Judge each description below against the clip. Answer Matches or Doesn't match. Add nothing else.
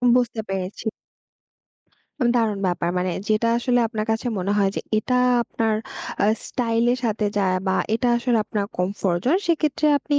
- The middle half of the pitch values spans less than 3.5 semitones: Doesn't match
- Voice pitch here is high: Matches